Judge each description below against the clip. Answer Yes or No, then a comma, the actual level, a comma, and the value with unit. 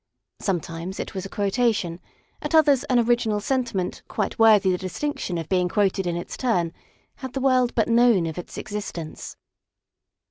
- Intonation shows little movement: No, average, 5.1 semitones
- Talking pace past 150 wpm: Yes, average, 165 wpm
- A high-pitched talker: Yes, high, 205 Hz